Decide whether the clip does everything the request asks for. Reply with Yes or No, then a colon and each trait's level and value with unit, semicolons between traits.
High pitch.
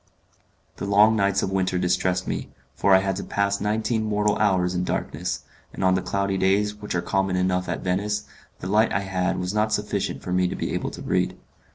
No: very low, 95 Hz